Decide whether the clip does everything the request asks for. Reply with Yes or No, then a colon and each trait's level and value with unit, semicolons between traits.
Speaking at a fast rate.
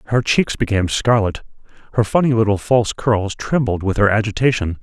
No: average, 160 wpm